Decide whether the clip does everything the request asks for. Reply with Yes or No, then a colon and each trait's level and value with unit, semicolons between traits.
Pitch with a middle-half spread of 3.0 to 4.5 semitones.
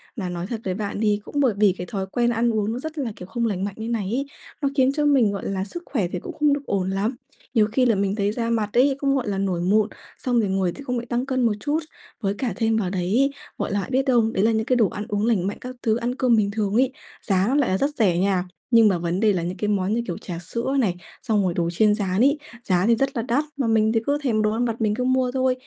Yes: average, 4.2 semitones